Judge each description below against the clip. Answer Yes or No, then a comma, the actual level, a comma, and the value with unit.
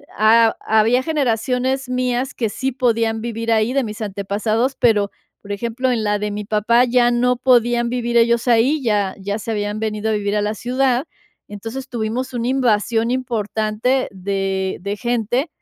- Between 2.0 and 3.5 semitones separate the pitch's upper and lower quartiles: Yes, average, 2.9 semitones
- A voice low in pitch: No, high, 230 Hz